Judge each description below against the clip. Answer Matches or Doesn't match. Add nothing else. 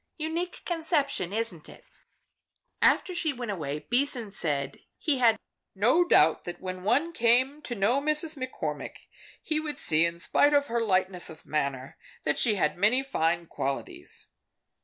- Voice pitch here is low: Doesn't match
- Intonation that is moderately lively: Doesn't match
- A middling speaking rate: Matches